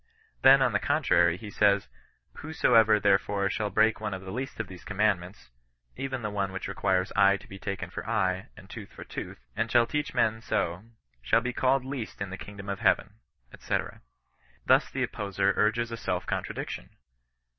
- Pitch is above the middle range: No, low, 105 Hz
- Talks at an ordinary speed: Yes, average, 190 wpm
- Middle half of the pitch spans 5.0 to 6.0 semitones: No, average, 3.1 semitones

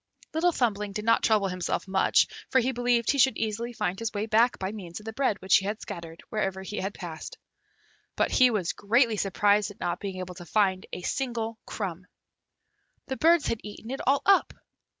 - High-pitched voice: Yes, high, 210 Hz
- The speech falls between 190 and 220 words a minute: Yes, fast, 205 wpm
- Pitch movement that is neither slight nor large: Yes, average, 3.9 semitones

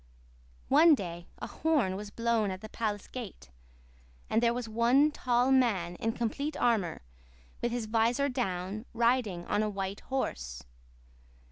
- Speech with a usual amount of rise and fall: Yes, average, 4.0 semitones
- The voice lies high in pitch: Yes, high, 225 Hz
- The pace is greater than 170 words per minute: No, average, 145 wpm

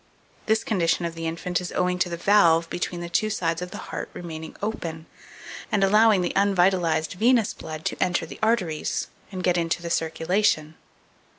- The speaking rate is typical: Yes, average, 180 wpm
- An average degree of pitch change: Yes, average, 3.1 semitones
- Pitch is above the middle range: No, medium, 175 Hz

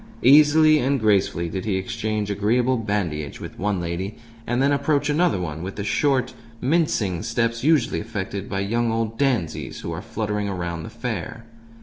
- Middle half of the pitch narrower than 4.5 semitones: No, average, 4.9 semitones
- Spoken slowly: No, average, 165 wpm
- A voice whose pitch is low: Yes, low, 110 Hz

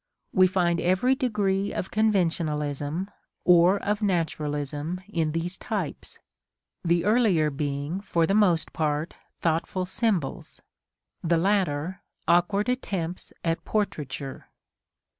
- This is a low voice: No, medium, 175 Hz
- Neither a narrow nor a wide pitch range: Yes, average, 3.9 semitones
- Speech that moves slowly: Yes, slow, 105 wpm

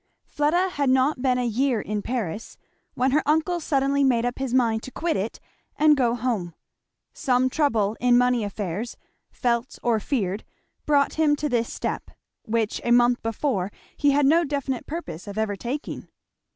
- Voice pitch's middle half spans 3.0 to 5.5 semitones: Yes, average, 4.0 semitones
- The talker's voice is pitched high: Yes, very high, 250 Hz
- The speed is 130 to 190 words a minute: Yes, average, 170 wpm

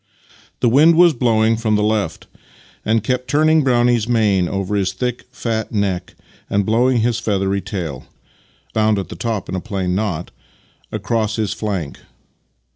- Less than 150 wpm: No, average, 165 wpm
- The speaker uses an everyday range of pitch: Yes, average, 3.4 semitones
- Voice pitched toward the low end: Yes, low, 110 Hz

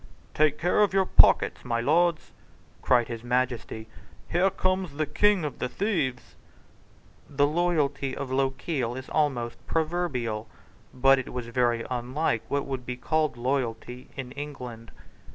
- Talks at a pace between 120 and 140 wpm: Yes, slow, 135 wpm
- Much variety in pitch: No, average, 4.2 semitones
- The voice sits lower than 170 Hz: Yes, low, 135 Hz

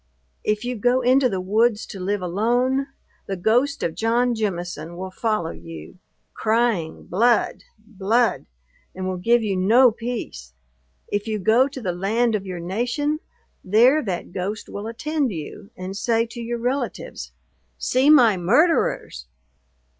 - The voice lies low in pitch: No, high, 220 Hz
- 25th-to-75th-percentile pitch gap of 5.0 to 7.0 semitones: No, average, 4.6 semitones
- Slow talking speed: No, average, 145 wpm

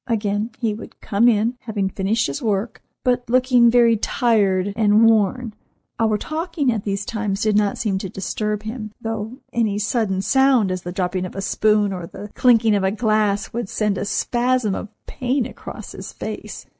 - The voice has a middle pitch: No, high, 215 Hz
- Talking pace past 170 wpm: Yes, average, 180 wpm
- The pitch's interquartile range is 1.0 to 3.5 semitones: Yes, average, 2.9 semitones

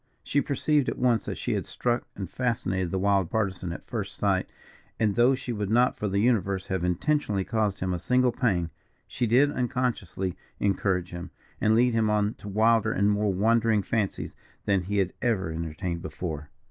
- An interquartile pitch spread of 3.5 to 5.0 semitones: Yes, average, 3.9 semitones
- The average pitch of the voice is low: Yes, low, 105 Hz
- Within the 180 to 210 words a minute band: Yes, average, 185 wpm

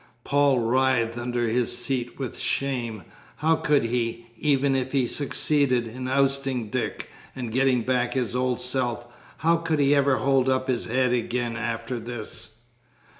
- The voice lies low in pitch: Yes, low, 125 Hz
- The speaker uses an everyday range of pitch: No, narrow, 2.2 semitones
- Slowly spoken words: No, average, 155 wpm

